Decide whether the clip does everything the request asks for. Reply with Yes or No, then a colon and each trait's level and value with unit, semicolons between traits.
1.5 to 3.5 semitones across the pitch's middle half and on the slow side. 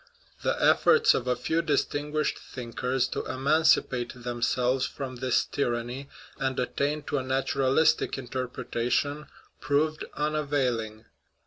Yes: average, 2.9 semitones; slow, 115 wpm